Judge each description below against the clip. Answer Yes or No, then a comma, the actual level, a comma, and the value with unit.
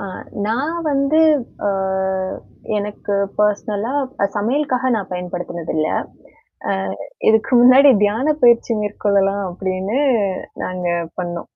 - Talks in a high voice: Yes, high, 210 Hz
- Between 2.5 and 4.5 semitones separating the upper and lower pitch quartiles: No, average, 5.0 semitones